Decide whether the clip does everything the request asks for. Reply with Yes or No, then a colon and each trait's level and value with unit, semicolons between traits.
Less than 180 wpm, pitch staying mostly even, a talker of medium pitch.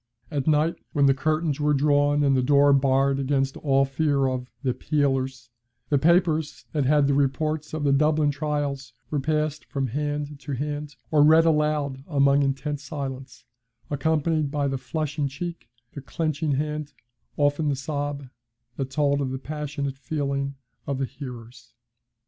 Yes: average, 160 wpm; narrow, 1.8 semitones; medium, 145 Hz